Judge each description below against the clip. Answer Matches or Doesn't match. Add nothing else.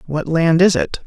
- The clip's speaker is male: Matches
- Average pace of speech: Doesn't match